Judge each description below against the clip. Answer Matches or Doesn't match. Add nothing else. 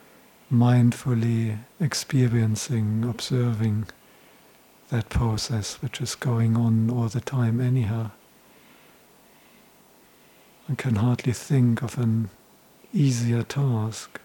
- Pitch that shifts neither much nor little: Doesn't match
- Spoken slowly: Matches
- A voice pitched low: Matches